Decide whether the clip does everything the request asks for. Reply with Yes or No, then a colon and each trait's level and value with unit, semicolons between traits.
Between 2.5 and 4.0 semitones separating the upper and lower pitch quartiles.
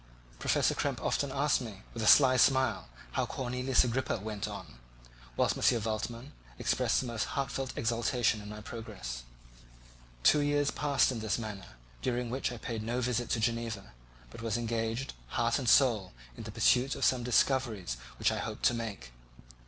Yes: average, 2.9 semitones